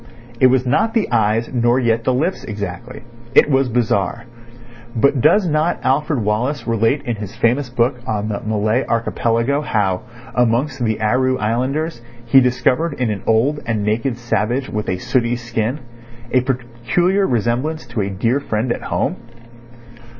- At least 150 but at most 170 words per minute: Yes, average, 155 wpm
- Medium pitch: No, low, 120 Hz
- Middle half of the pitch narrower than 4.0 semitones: Yes, average, 3.1 semitones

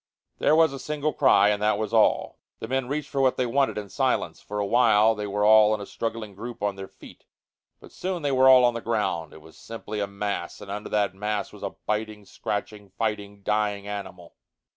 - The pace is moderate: No, fast, 225 wpm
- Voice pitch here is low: Yes, low, 105 Hz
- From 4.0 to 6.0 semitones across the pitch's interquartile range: No, average, 3.0 semitones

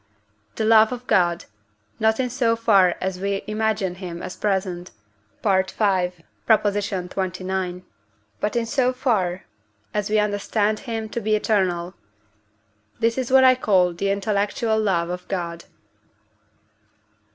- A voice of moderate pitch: No, high, 200 Hz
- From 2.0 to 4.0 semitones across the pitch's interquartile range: Yes, average, 3.2 semitones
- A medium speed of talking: No, slow, 130 wpm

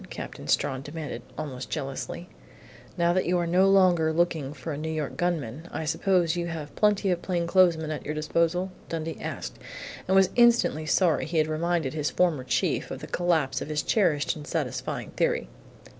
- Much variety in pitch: No, narrow, 2.6 semitones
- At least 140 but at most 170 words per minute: No, average, 180 wpm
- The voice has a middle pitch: Yes, medium, 165 Hz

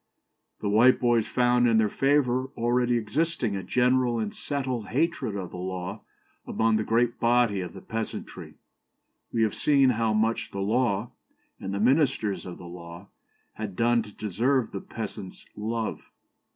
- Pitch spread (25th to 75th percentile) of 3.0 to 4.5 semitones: Yes, average, 3.3 semitones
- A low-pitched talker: Yes, low, 115 Hz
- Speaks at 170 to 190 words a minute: No, average, 155 wpm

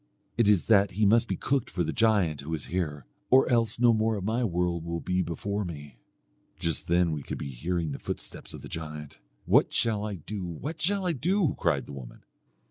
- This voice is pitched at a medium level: No, very low, 90 Hz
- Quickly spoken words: Yes, fast, 215 wpm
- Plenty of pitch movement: Yes, wide, 5.8 semitones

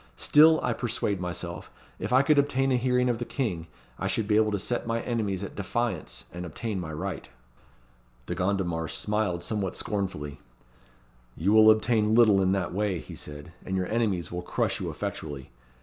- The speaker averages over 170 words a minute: Yes, average, 180 wpm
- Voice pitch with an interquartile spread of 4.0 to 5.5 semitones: Yes, average, 4.7 semitones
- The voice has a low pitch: Yes, low, 100 Hz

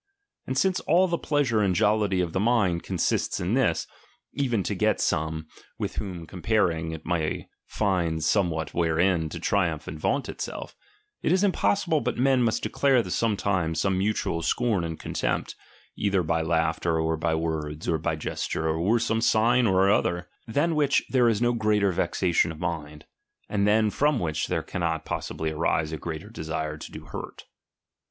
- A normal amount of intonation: No, wide, 5.9 semitones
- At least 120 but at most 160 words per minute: No, average, 175 wpm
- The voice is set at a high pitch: No, very low, 95 Hz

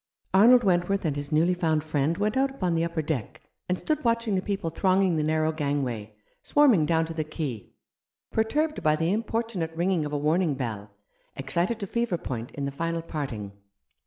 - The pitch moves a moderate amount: Yes, average, 4.9 semitones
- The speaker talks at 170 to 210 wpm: Yes, average, 190 wpm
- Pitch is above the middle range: No, medium, 165 Hz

